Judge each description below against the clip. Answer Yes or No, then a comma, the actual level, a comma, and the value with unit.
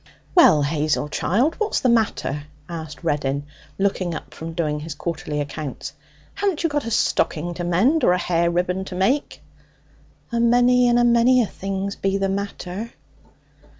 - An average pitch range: No, wide, 6.7 semitones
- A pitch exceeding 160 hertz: Yes, high, 190 Hz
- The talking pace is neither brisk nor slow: Yes, average, 160 wpm